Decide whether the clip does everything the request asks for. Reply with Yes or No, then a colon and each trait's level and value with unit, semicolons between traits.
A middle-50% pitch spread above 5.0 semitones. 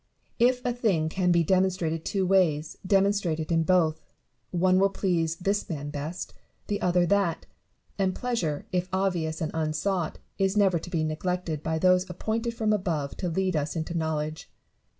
No: average, 3.4 semitones